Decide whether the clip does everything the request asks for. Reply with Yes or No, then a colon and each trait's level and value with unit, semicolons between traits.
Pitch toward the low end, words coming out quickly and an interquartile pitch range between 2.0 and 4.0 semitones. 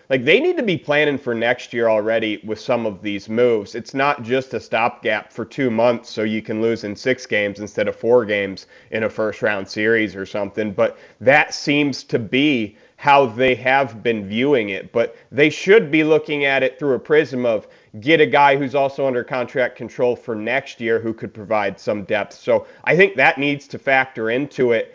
No: low, 125 Hz; fast, 210 wpm; average, 4.4 semitones